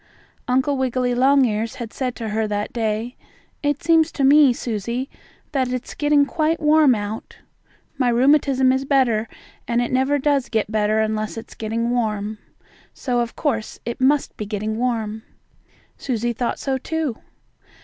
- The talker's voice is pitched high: Yes, high, 245 Hz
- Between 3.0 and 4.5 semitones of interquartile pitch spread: Yes, average, 3.8 semitones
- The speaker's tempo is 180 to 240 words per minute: No, average, 155 wpm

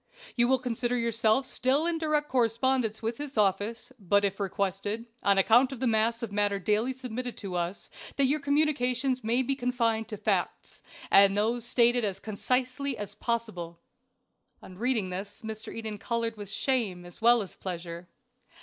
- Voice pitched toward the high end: Yes, high, 230 Hz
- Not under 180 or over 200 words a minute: No, average, 170 wpm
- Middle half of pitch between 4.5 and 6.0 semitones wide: No, average, 3.8 semitones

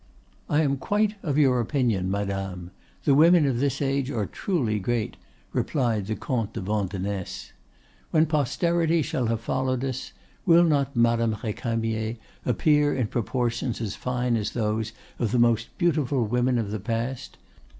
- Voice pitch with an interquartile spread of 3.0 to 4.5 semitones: Yes, average, 4.2 semitones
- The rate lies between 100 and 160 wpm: Yes, average, 150 wpm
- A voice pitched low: Yes, low, 120 Hz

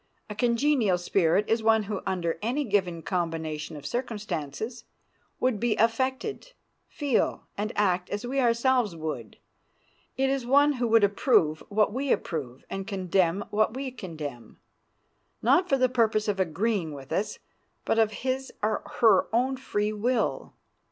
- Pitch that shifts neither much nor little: No, wide, 5.7 semitones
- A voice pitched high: Yes, high, 215 Hz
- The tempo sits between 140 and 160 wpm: Yes, average, 150 wpm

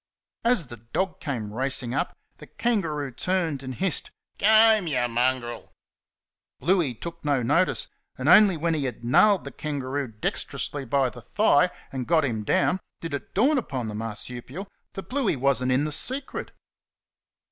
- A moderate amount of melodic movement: No, wide, 6.8 semitones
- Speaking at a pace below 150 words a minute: No, average, 165 wpm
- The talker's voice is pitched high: No, medium, 145 Hz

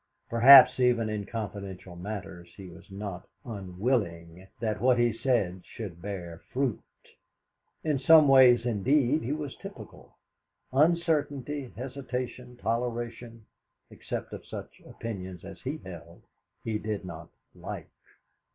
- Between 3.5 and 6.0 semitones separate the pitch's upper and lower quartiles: Yes, average, 5.2 semitones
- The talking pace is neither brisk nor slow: No, slow, 120 wpm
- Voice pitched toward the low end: Yes, low, 115 Hz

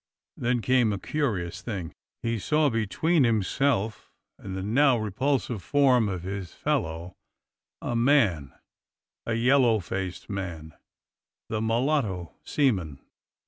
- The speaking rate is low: Yes, slow, 125 wpm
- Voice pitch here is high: No, low, 110 Hz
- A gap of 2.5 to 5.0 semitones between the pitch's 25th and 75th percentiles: No, wide, 5.5 semitones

